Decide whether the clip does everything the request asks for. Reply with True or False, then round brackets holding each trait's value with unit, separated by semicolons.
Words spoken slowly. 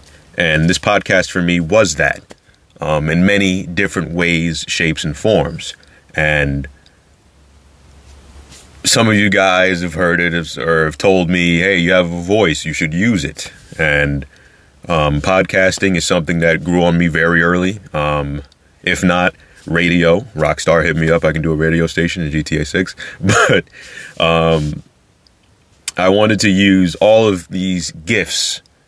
False (155 wpm)